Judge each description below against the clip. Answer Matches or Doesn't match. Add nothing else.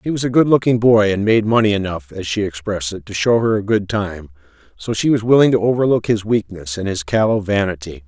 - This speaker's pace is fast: Matches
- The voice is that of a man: Matches